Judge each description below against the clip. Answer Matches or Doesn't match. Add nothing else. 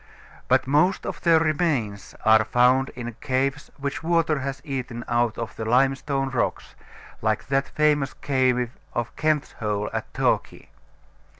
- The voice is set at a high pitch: Doesn't match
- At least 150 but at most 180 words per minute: Doesn't match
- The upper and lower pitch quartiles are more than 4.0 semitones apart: Doesn't match